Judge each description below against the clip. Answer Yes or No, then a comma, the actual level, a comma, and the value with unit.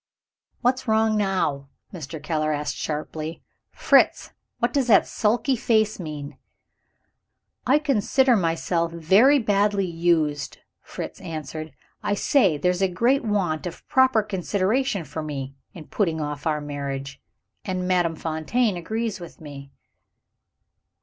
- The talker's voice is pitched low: No, medium, 180 Hz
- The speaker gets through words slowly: Yes, slow, 125 wpm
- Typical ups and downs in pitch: No, wide, 5.9 semitones